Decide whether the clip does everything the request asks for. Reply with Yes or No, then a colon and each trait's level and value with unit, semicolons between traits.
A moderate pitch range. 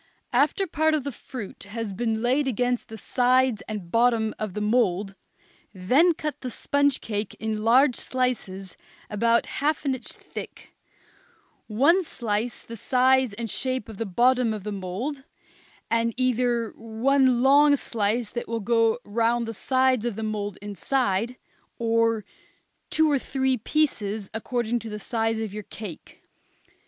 Yes: average, 3.3 semitones